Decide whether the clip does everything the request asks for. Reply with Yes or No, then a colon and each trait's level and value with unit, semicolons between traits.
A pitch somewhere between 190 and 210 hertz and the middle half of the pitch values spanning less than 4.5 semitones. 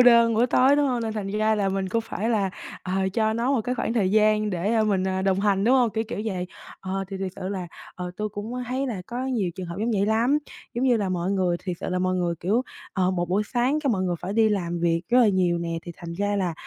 Yes: high, 205 Hz; average, 3.8 semitones